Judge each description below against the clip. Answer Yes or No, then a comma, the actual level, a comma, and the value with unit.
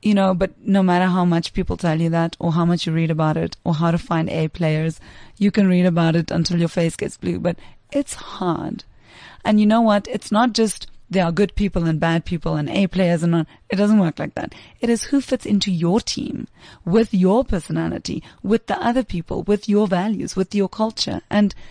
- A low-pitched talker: No, medium, 185 Hz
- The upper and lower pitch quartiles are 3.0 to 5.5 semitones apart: Yes, average, 3.8 semitones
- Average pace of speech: No, fast, 225 wpm